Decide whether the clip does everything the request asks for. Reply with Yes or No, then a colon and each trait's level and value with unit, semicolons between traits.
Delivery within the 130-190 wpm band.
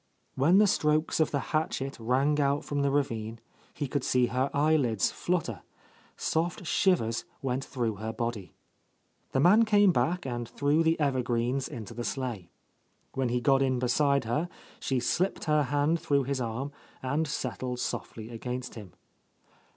Yes: average, 160 wpm